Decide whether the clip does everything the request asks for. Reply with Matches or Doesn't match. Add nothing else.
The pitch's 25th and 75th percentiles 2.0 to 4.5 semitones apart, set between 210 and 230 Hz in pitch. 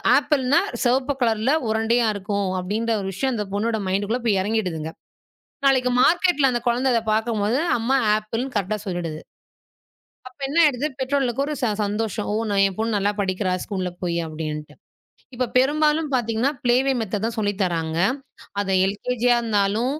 Matches